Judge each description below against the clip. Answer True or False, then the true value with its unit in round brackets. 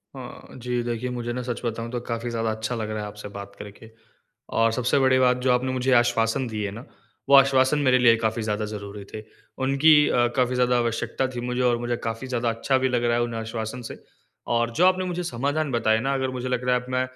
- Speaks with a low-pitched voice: True (120 Hz)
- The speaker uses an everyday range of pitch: False (2.2 semitones)